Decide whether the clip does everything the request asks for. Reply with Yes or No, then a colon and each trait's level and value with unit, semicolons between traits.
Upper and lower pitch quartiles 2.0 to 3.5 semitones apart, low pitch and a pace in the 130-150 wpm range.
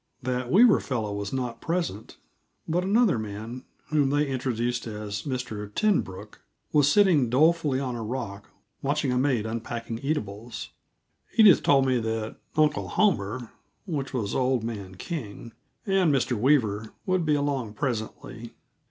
No: average, 5.0 semitones; low, 125 Hz; average, 140 wpm